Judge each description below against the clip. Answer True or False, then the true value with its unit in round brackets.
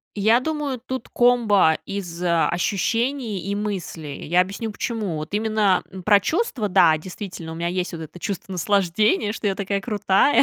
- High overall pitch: True (200 Hz)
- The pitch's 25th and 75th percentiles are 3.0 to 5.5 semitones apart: True (3.7 semitones)